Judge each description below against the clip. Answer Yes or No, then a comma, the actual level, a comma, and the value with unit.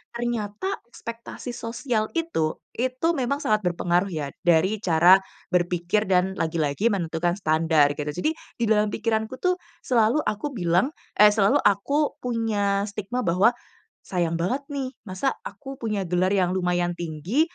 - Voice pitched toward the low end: No, high, 205 Hz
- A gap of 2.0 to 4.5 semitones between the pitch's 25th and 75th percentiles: No, average, 5.3 semitones